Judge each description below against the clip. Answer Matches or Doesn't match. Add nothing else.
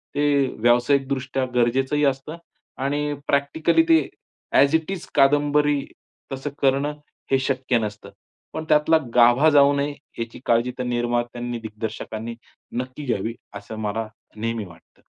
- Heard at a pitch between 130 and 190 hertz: Matches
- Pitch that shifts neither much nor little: Matches